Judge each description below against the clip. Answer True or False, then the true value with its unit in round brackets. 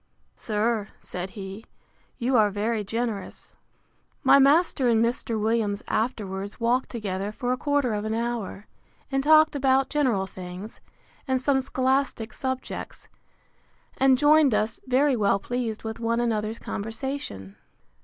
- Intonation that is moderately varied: True (3.8 semitones)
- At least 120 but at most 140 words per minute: True (135 wpm)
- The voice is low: False (230 Hz)